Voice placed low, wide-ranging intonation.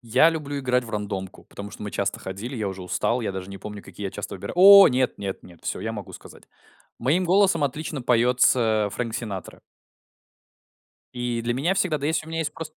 Yes: low, 125 Hz; wide, 6.7 semitones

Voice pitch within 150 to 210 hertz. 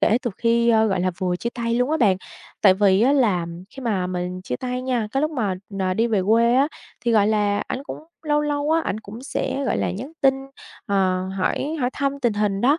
No: high, 230 Hz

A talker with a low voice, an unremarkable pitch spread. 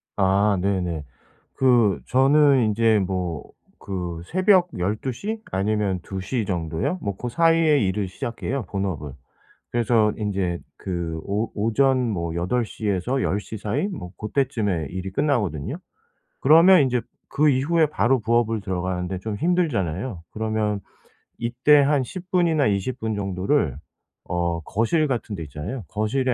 No: low, 110 Hz; wide, 6.1 semitones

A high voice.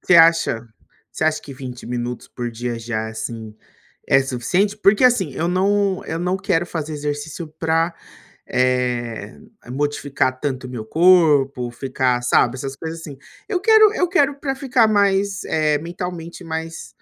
No: medium, 155 Hz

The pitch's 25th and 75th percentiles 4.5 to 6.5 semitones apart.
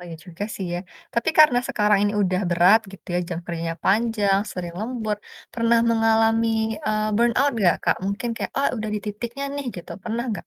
No: average, 3.3 semitones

